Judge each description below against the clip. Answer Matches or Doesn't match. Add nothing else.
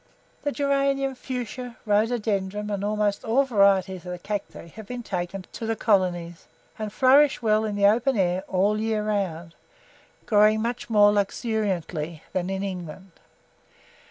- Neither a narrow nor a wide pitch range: Matches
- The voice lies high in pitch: Matches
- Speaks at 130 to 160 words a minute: Matches